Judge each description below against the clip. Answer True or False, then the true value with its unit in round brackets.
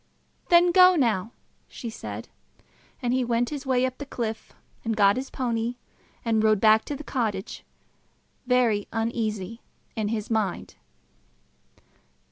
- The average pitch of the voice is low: False (230 Hz)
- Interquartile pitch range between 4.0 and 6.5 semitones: False (2.8 semitones)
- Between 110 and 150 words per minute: True (135 wpm)